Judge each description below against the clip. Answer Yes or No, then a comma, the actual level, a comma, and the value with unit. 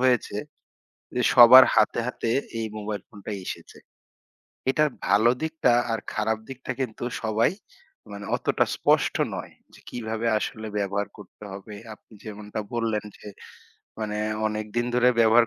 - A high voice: No, low, 110 Hz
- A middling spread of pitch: No, narrow, 2.3 semitones